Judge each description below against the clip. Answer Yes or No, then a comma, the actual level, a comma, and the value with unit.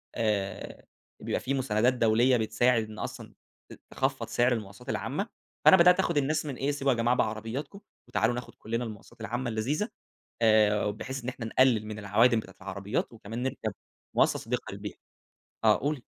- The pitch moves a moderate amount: Yes, average, 3.4 semitones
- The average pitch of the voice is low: Yes, low, 120 Hz